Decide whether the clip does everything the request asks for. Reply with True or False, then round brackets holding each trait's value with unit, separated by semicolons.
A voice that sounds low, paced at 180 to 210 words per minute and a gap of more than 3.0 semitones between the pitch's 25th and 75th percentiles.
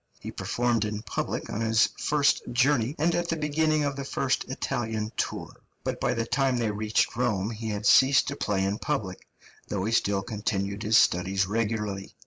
True (110 Hz; 185 wpm; 4.5 semitones)